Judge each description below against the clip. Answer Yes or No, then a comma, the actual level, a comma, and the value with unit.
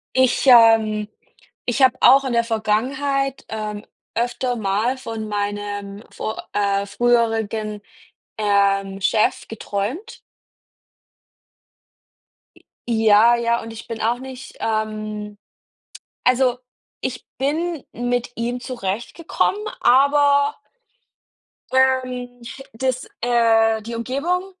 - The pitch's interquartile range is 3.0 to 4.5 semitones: Yes, average, 3.3 semitones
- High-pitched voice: Yes, high, 235 Hz